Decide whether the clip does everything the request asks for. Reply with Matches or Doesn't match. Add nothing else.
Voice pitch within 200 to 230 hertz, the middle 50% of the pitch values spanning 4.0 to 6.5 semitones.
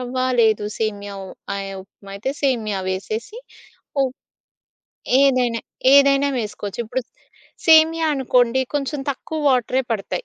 Doesn't match